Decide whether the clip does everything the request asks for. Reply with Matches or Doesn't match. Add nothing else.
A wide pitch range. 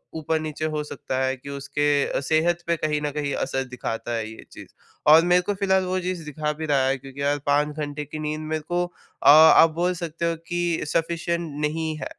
Doesn't match